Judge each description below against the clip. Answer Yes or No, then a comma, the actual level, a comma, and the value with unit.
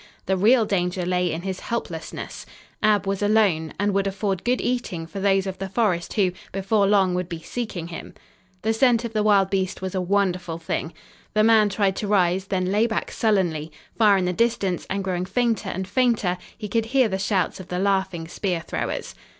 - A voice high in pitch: Yes, high, 195 Hz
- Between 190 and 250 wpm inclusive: Yes, average, 200 wpm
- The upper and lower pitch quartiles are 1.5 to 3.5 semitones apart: Yes, average, 2.8 semitones